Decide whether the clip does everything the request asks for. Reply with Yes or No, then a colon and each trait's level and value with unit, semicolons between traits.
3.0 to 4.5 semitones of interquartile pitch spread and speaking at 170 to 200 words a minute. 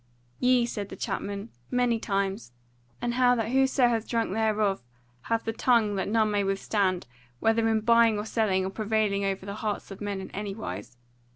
No: narrow, 2.6 semitones; average, 185 wpm